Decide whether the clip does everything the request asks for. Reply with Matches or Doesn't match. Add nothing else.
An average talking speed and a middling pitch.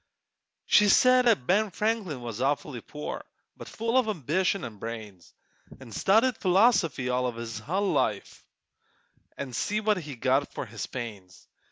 Matches